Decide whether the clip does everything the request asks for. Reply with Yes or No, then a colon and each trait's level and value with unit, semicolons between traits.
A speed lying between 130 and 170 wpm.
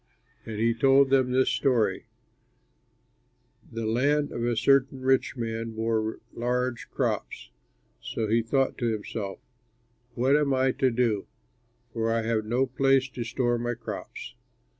Yes: average, 140 wpm